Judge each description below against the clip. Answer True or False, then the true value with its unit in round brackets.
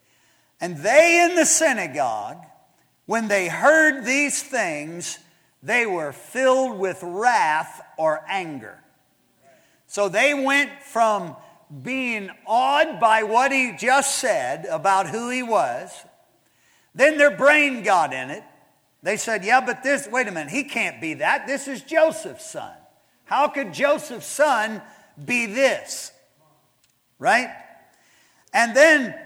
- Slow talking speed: True (130 wpm)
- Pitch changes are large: True (6.0 semitones)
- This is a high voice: True (255 Hz)